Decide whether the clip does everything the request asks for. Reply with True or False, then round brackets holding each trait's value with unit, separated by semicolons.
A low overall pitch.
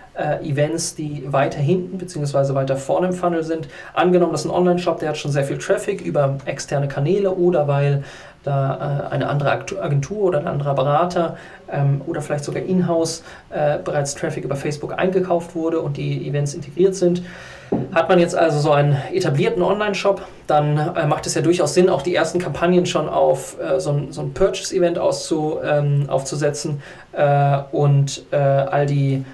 False (160 Hz)